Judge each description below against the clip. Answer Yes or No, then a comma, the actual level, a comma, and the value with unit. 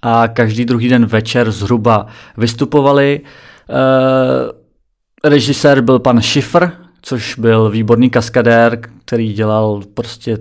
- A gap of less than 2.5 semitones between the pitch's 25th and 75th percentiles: No, average, 2.8 semitones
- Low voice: Yes, low, 120 Hz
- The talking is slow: Yes, slow, 110 wpm